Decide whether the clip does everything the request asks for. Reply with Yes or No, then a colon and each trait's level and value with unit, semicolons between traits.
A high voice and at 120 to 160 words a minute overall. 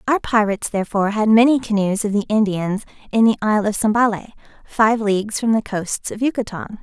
No: high, 215 Hz; average, 185 wpm